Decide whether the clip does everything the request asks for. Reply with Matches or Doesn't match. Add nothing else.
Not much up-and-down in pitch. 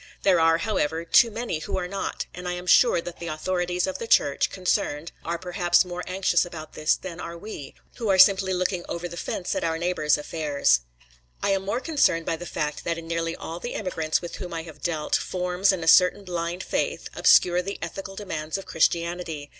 Matches